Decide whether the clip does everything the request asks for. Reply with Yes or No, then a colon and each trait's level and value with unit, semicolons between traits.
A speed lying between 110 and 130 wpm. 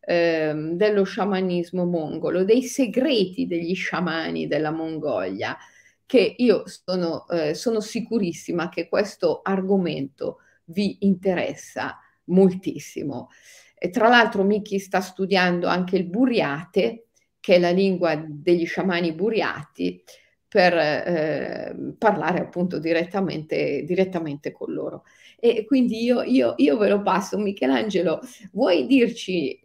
Yes: slow, 115 wpm